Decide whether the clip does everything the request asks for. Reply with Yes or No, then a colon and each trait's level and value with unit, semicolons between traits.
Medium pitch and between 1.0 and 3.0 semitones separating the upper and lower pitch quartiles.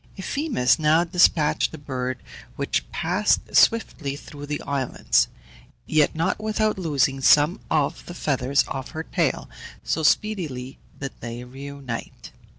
No: medium, 145 Hz; average, 4.4 semitones